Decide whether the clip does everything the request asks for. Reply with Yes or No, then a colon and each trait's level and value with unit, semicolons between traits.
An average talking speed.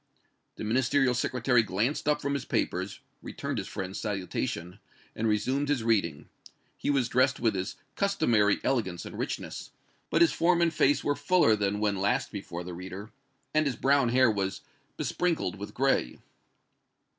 Yes: average, 160 wpm